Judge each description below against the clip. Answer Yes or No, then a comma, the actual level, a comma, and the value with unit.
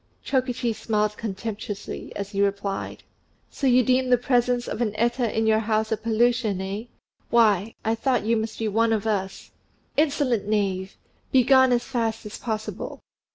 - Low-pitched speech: No, high, 225 Hz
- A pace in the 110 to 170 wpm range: Yes, average, 160 wpm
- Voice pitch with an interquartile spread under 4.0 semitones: Yes, narrow, 2.6 semitones